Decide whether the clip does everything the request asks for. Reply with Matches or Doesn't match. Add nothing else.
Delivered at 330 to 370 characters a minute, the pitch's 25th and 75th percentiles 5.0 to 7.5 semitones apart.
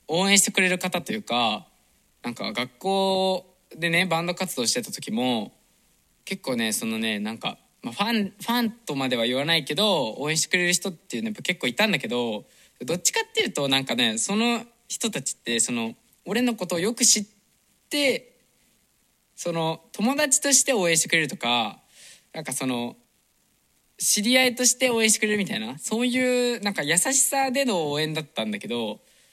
Matches